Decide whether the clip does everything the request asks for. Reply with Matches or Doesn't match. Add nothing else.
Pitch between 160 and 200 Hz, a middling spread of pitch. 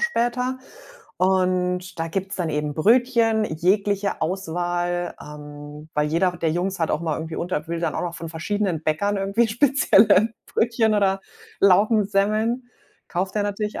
Matches